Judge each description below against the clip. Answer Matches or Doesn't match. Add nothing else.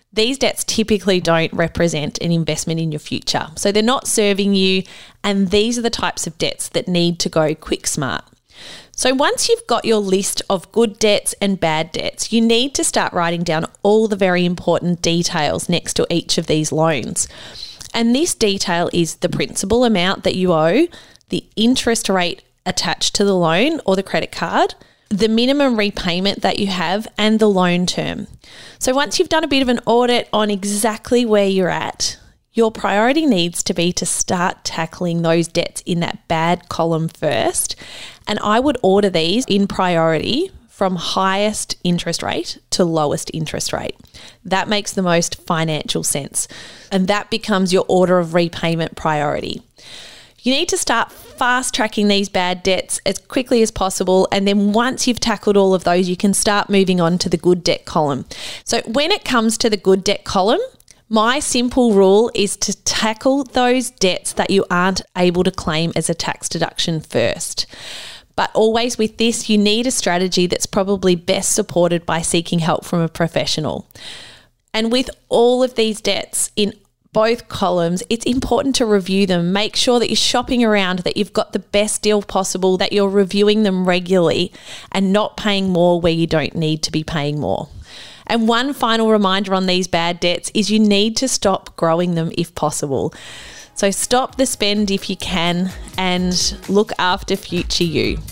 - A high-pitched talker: Matches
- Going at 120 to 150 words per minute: Doesn't match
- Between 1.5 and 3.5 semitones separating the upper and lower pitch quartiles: Doesn't match